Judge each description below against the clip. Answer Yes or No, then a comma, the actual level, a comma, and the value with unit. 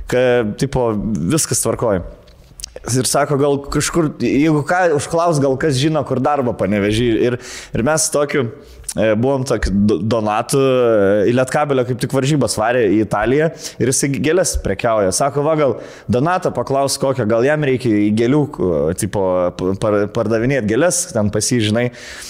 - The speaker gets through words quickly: No, slow, 135 wpm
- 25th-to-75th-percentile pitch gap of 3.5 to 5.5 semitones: Yes, average, 4.2 semitones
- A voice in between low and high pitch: No, low, 130 Hz